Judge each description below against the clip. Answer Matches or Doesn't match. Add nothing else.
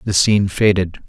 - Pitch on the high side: Doesn't match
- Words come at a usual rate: Matches